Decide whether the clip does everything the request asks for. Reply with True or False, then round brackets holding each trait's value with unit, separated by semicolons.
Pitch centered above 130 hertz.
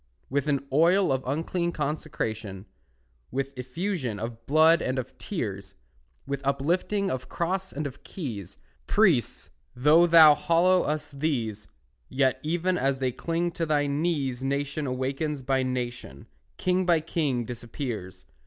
True (140 Hz)